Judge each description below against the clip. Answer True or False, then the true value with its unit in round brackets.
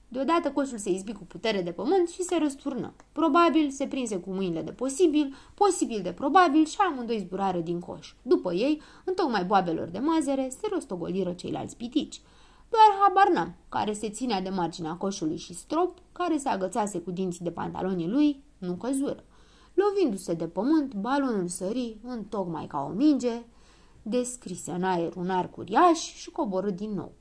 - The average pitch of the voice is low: False (240 Hz)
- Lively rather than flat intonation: True (8.8 semitones)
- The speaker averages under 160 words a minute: False (170 wpm)